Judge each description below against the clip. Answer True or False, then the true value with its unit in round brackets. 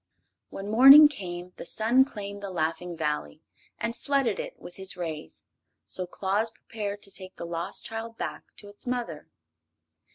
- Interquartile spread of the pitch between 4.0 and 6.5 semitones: True (4.6 semitones)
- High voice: True (200 Hz)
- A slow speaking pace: False (160 wpm)